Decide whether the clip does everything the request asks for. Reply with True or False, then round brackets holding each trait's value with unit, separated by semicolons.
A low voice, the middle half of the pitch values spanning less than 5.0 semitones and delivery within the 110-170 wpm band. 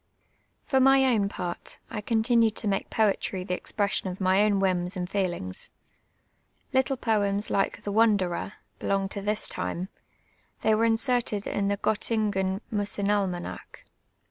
False (205 Hz; 2.5 semitones; 155 wpm)